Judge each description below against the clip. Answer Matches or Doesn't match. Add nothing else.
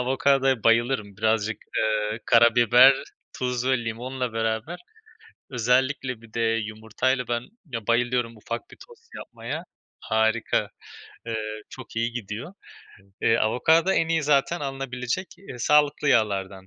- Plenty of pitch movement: Doesn't match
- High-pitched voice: Doesn't match